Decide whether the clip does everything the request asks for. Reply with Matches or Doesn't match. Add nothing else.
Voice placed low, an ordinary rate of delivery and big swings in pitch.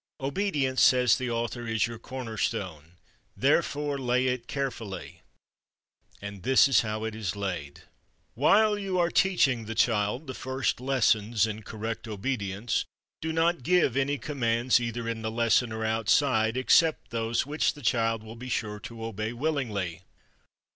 Doesn't match